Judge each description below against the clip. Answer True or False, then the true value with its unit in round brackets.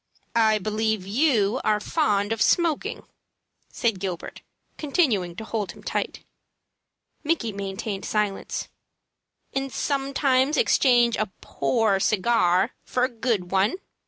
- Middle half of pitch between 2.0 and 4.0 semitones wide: False (4.8 semitones)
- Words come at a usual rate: False (115 wpm)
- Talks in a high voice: True (220 Hz)